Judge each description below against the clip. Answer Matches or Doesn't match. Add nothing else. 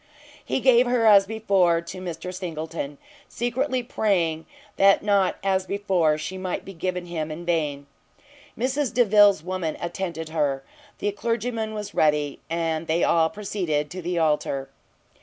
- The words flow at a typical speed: Matches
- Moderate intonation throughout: Matches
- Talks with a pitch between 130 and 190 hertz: Matches